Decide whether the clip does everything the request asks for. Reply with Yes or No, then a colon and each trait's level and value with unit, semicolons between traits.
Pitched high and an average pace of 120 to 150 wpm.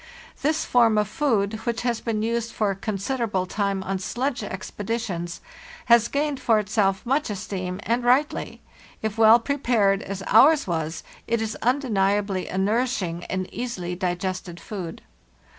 Yes: high, 215 Hz; average, 145 wpm